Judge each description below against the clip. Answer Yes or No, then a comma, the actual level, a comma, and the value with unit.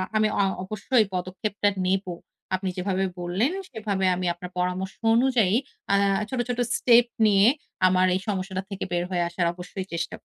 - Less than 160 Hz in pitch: No, high, 190 Hz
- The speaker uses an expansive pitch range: No, average, 2.8 semitones